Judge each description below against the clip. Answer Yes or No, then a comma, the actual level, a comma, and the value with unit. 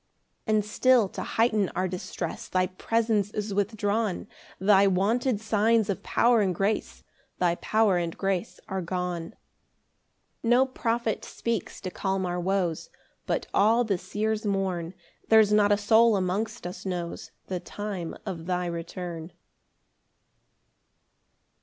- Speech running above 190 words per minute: No, slow, 135 wpm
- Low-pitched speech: No, high, 200 Hz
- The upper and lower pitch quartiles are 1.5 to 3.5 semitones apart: Yes, average, 3.2 semitones